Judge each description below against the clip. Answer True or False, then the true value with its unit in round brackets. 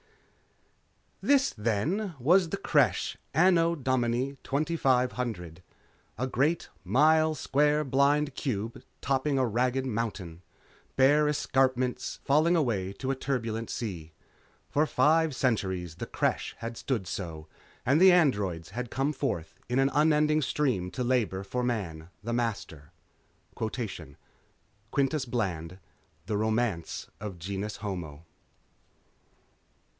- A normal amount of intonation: False (6.1 semitones)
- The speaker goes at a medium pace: False (115 wpm)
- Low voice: True (125 Hz)